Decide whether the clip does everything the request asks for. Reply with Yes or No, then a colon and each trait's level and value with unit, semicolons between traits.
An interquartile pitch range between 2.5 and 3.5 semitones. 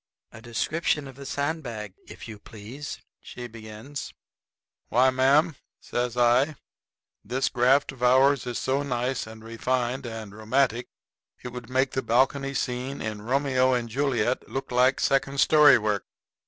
Yes: average, 2.8 semitones